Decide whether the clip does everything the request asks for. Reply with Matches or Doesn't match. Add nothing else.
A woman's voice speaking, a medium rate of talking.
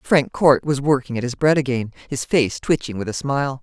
Doesn't match